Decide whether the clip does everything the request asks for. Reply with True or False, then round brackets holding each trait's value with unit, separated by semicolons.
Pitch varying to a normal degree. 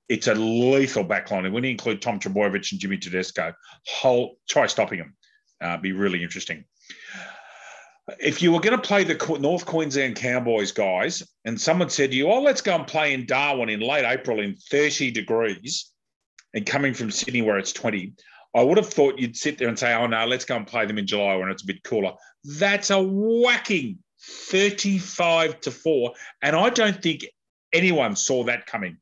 False (7.4 semitones)